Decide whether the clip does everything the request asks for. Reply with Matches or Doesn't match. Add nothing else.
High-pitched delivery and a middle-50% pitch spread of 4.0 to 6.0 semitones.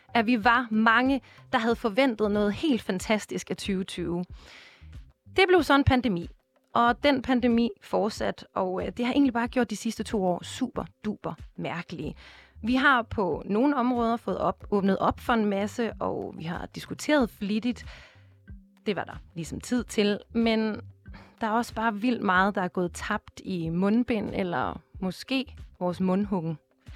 Matches